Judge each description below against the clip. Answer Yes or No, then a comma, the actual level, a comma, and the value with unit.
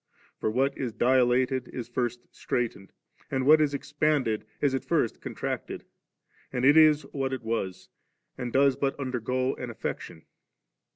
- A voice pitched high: No, low, 130 Hz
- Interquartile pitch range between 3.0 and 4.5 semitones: No, narrow, 2.5 semitones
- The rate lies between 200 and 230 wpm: No, average, 150 wpm